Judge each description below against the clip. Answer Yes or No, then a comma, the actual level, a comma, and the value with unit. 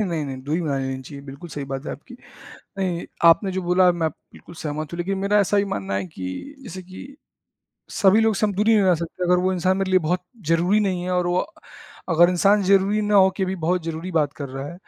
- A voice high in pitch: No, medium, 180 Hz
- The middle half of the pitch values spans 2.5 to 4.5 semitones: Yes, average, 3.7 semitones